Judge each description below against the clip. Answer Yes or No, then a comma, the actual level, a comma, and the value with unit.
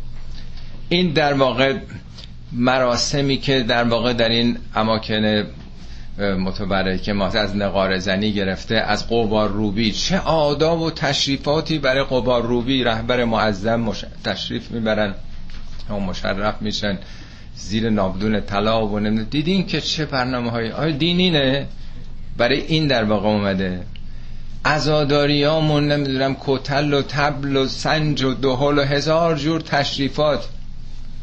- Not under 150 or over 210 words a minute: No, average, 125 wpm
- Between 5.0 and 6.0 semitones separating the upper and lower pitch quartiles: Yes, wide, 5.4 semitones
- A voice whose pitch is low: Yes, low, 120 Hz